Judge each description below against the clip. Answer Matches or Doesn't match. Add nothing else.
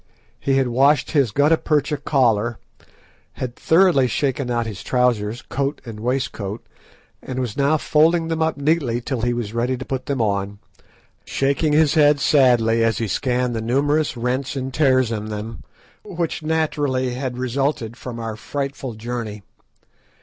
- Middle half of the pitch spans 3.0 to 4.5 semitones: Matches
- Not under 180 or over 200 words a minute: Doesn't match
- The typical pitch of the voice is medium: Doesn't match